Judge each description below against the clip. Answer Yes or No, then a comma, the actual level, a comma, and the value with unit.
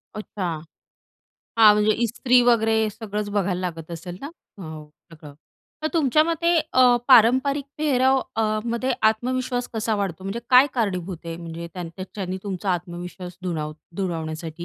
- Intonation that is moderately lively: No, wide, 6.0 semitones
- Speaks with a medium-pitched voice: No, high, 210 Hz